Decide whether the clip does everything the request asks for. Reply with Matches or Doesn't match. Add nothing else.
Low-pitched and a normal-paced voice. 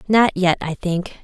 Doesn't match